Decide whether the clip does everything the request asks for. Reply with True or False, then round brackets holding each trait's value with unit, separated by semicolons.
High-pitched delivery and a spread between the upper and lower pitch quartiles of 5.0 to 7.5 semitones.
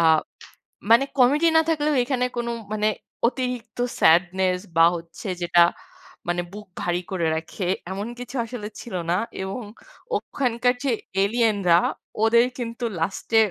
True (220 Hz; 5.5 semitones)